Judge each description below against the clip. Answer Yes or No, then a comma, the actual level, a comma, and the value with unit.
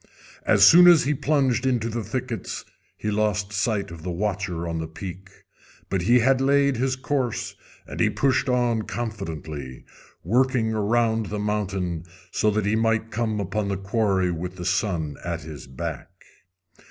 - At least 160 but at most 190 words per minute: Yes, average, 165 wpm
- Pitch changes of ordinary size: Yes, average, 4.7 semitones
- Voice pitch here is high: No, low, 105 Hz